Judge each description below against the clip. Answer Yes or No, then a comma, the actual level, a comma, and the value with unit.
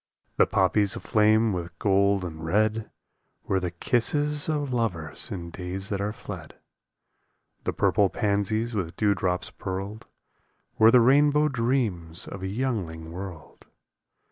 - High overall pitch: No, low, 100 Hz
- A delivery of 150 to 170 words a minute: No, slow, 135 wpm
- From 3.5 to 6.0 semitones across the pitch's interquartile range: Yes, average, 4.1 semitones